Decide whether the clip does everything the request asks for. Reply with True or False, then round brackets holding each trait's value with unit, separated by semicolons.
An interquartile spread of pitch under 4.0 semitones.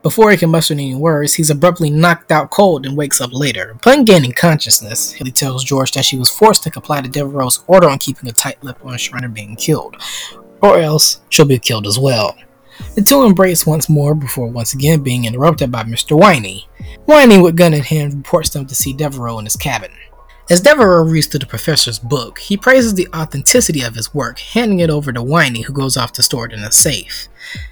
False (5.0 semitones)